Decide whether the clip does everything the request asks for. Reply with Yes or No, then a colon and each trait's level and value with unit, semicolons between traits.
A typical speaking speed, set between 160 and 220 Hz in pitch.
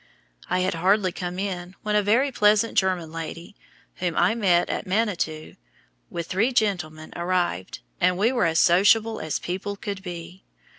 Yes: average, 160 wpm; medium, 185 Hz